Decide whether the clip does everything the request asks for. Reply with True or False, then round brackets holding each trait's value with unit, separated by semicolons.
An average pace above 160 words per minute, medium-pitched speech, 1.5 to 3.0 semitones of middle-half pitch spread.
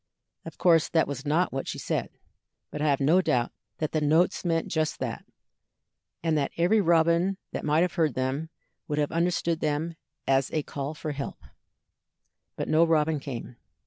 True (175 wpm; 155 Hz; 2.6 semitones)